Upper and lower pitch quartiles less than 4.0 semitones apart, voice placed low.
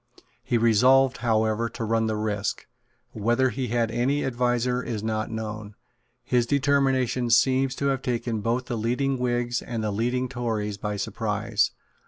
Yes: narrow, 2.5 semitones; low, 120 Hz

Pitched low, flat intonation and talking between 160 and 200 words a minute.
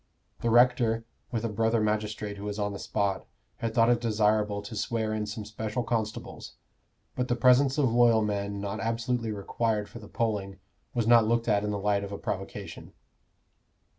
Yes: low, 110 Hz; narrow, 2.1 semitones; average, 185 wpm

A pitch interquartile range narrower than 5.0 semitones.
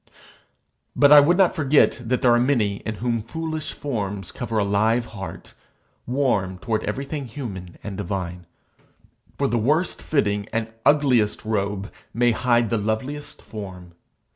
No: wide, 5.4 semitones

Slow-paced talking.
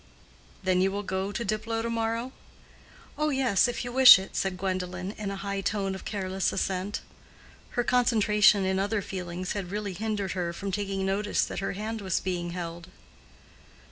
No: average, 175 wpm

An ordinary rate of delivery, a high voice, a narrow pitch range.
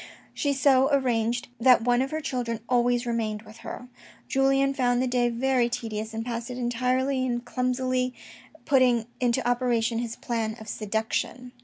Yes: average, 165 wpm; high, 245 Hz; narrow, 1.8 semitones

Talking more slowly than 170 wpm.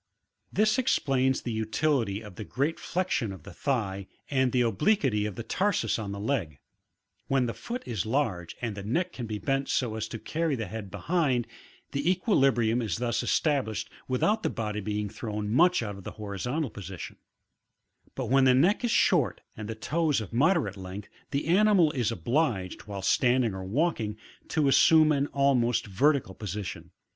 No: average, 175 wpm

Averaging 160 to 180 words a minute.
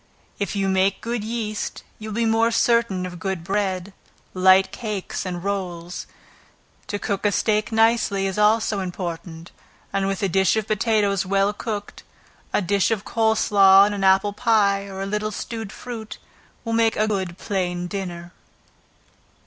Yes: average, 165 wpm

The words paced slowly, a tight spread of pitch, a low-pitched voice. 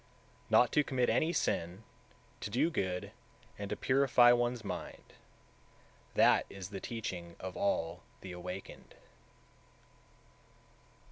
No: slow, 120 wpm; wide, 5.4 semitones; low, 105 Hz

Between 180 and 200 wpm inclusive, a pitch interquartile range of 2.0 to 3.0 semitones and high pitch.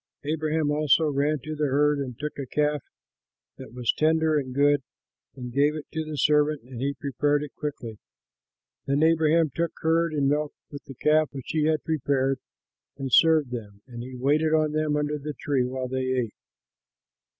No: average, 185 wpm; narrow, 2.6 semitones; medium, 145 Hz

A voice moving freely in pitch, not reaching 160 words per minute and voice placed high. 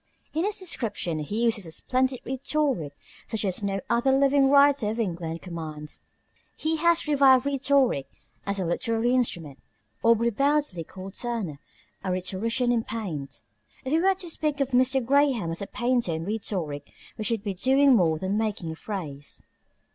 No: wide, 7.0 semitones; average, 165 wpm; high, 230 Hz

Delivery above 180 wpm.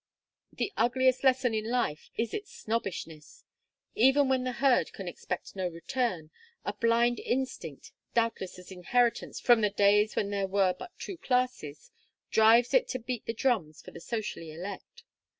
No: average, 160 wpm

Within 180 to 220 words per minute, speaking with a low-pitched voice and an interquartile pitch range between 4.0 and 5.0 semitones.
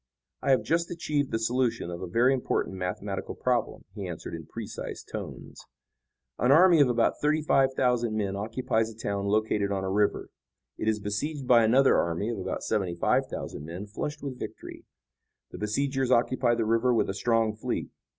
Yes: average, 185 wpm; low, 115 Hz; average, 4.4 semitones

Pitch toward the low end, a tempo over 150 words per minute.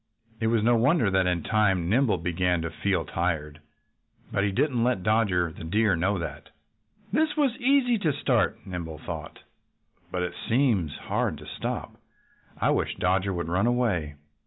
Yes: very low, 95 Hz; average, 165 wpm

